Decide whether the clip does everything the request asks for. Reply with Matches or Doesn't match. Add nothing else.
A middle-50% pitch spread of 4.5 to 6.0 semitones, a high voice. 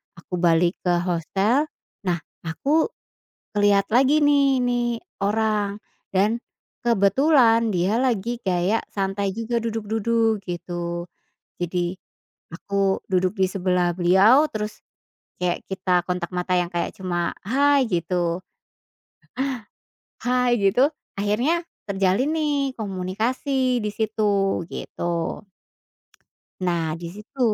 Matches